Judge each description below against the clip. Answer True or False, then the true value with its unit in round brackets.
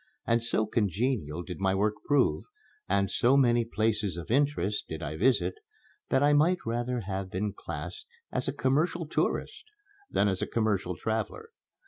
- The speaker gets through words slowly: False (160 wpm)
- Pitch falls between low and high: False (110 Hz)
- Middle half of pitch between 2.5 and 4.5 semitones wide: False (5.3 semitones)